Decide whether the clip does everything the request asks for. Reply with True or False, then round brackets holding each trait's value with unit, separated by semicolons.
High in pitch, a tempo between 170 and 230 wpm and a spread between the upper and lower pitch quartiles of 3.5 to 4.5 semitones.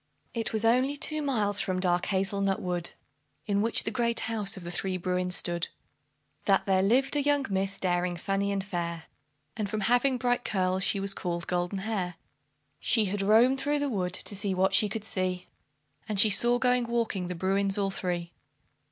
True (195 Hz; 190 wpm; 3.8 semitones)